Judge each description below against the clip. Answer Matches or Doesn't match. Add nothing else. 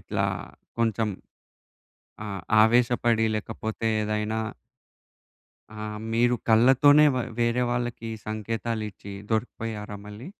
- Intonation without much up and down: Matches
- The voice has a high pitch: Doesn't match